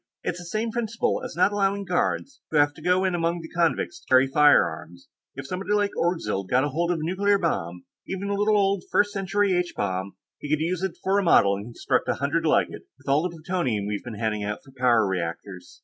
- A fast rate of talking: Yes, fast, 230 wpm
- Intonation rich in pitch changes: Yes, wide, 8.8 semitones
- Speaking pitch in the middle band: Yes, medium, 165 Hz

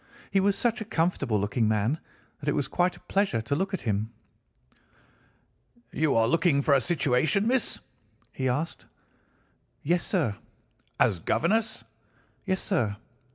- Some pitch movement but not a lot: No, wide, 8.3 semitones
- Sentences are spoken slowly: No, average, 145 wpm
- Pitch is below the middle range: No, medium, 150 Hz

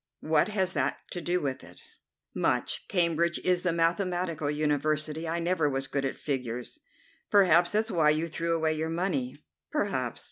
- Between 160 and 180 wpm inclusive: Yes, average, 165 wpm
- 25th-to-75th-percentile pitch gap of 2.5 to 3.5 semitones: Yes, average, 2.9 semitones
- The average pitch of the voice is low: No, medium, 165 Hz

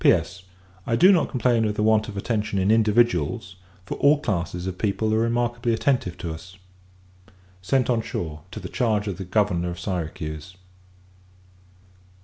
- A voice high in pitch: No, low, 105 Hz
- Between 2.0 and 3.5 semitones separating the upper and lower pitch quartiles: No, average, 4.3 semitones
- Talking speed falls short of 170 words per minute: Yes, average, 160 wpm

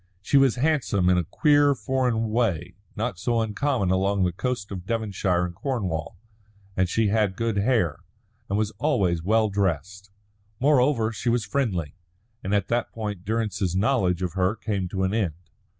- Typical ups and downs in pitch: Yes, average, 4.2 semitones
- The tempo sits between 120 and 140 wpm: No, average, 165 wpm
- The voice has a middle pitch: No, low, 105 Hz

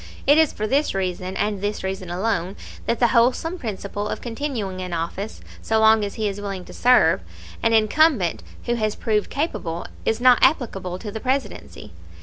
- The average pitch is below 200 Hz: No, high, 215 Hz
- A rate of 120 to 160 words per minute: No, average, 180 wpm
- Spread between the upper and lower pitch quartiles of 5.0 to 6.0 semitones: No, average, 4.2 semitones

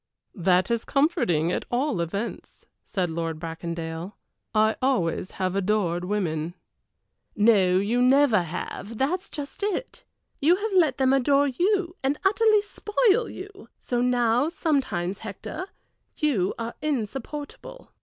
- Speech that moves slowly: Yes, slow, 130 wpm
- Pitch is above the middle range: Yes, high, 240 Hz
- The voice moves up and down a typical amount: No, wide, 8.6 semitones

